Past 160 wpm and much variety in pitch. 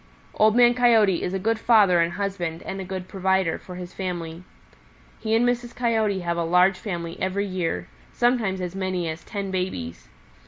No: average, 185 wpm; average, 3.6 semitones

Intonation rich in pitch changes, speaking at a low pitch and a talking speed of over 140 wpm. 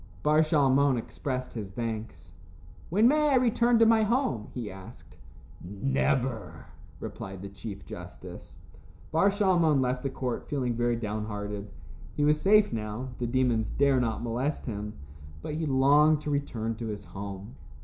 Yes: wide, 6.0 semitones; low, 125 Hz; average, 150 wpm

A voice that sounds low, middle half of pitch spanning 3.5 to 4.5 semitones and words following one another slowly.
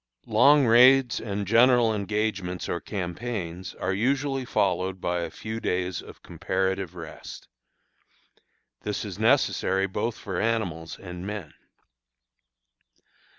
Yes: low, 100 Hz; average, 4.2 semitones; slow, 110 wpm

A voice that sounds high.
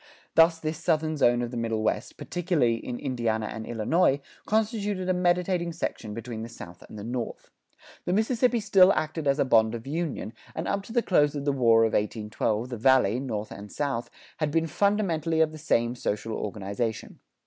No: medium, 140 Hz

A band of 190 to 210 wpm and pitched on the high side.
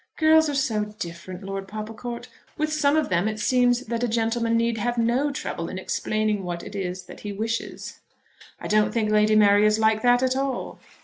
Yes: average, 200 wpm; high, 220 Hz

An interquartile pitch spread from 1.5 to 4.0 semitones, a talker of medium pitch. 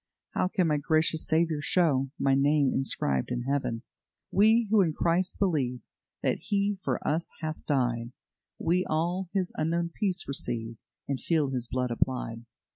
No: average, 5.1 semitones; medium, 155 Hz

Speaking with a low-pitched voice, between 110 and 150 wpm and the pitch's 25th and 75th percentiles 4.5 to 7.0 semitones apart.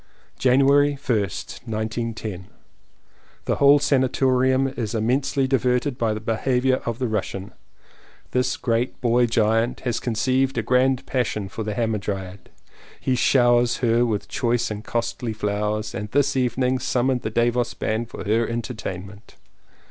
No: low, 120 Hz; average, 140 wpm; average, 2.9 semitones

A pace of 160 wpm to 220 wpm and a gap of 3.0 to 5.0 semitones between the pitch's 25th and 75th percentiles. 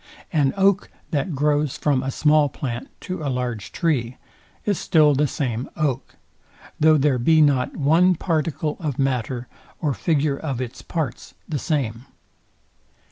No: average, 145 wpm; average, 3.4 semitones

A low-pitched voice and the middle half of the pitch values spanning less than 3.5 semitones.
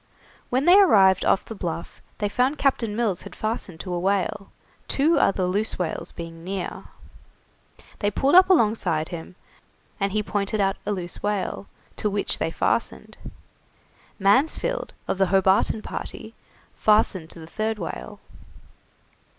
No: high, 200 Hz; average, 3.1 semitones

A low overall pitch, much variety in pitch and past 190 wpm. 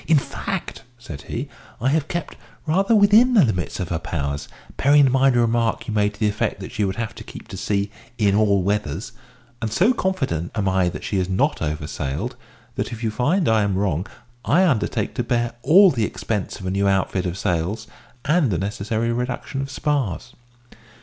Yes: low, 110 Hz; wide, 6.0 semitones; fast, 205 wpm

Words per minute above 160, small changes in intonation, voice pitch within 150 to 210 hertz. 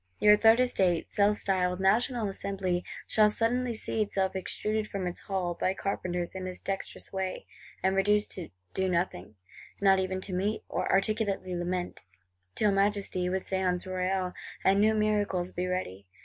No: average, 155 wpm; narrow, 2.3 semitones; high, 190 Hz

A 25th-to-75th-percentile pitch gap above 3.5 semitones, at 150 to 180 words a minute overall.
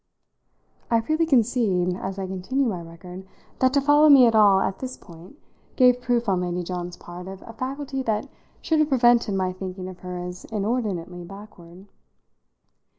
Yes: wide, 5.6 semitones; average, 170 wpm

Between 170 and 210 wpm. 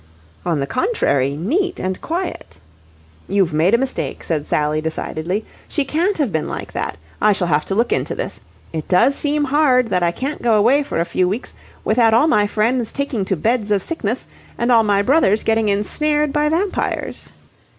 Yes: average, 190 wpm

